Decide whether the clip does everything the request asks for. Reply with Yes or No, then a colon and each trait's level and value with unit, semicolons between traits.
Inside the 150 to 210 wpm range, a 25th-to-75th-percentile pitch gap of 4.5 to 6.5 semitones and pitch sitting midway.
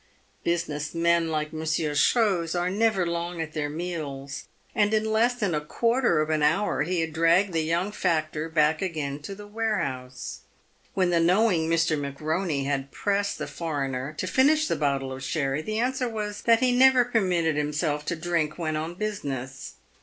Yes: average, 175 wpm; average, 5.0 semitones; medium, 165 Hz